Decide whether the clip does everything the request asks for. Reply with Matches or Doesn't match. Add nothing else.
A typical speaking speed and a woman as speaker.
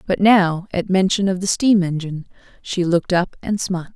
Matches